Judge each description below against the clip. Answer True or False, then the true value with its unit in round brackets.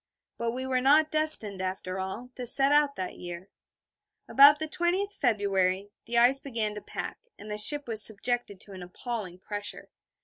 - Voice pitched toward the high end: True (230 Hz)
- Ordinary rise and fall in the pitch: False (5.8 semitones)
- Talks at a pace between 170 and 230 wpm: True (175 wpm)